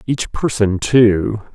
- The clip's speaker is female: No, male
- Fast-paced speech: No, slow, 115 wpm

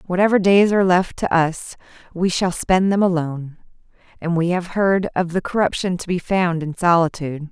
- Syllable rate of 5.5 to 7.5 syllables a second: No, 5.2 syllables/s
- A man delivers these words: No, female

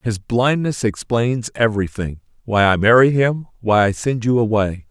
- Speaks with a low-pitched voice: Yes, low, 110 Hz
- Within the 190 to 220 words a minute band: No, average, 145 wpm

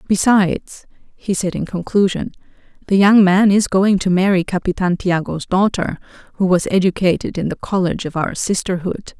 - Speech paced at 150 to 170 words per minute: Yes, average, 155 wpm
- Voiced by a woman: Yes, female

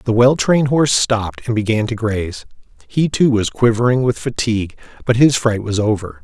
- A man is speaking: Yes, male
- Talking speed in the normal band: Yes, average, 195 wpm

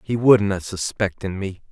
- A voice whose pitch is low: Yes, low, 100 Hz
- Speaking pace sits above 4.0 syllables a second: No, 3.9 syllables/s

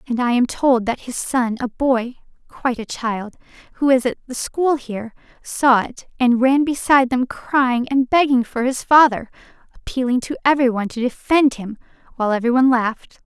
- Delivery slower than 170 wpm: No, average, 185 wpm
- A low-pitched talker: No, very high, 250 Hz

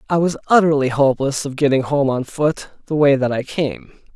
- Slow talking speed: No, average, 200 wpm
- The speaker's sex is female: No, male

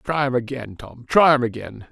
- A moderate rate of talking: No, fast, 220 wpm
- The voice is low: Yes, low, 125 Hz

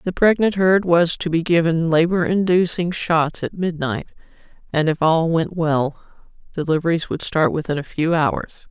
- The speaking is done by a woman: Yes, female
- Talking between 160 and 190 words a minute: Yes, average, 165 wpm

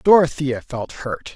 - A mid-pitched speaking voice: Yes, medium, 145 Hz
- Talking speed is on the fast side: No, slow, 135 wpm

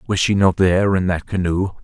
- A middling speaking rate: No, fast, 230 wpm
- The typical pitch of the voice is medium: No, very low, 95 Hz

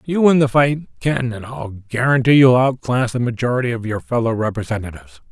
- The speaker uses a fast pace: No, average, 180 wpm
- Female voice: No, male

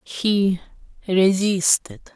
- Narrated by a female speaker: Yes, female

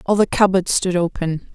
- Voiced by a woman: Yes, female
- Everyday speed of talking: Yes, average, 195 wpm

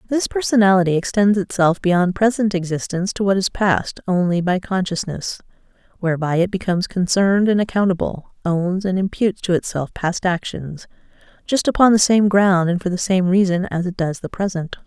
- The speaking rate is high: No, average, 165 wpm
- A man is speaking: No, female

